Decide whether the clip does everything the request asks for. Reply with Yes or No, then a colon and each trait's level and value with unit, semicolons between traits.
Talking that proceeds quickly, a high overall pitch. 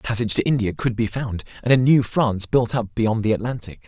No: fast, 250 wpm; low, 115 Hz